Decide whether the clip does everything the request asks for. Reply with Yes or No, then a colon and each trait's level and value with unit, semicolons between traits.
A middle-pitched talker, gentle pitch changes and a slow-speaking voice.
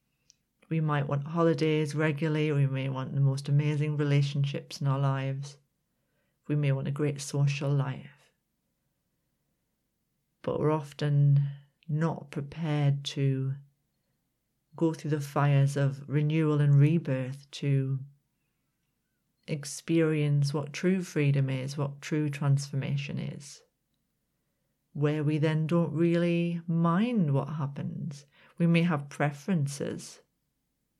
Yes: medium, 145 Hz; narrow, 2.1 semitones; slow, 110 wpm